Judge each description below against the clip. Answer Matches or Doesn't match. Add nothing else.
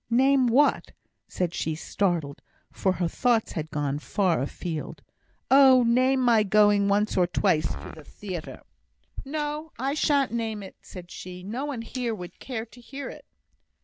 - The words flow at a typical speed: Matches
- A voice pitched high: Matches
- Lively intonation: Matches